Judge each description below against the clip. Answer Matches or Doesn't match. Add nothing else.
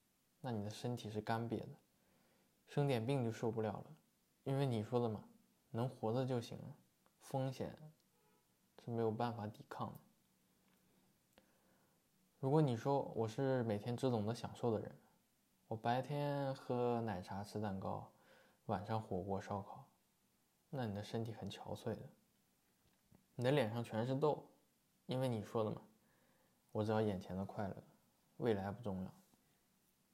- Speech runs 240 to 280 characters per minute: Doesn't match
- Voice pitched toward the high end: Doesn't match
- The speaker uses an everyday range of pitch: Matches